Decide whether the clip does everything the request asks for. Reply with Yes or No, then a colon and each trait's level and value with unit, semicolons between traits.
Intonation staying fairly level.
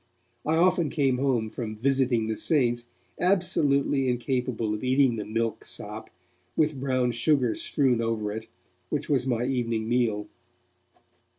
No: average, 3.4 semitones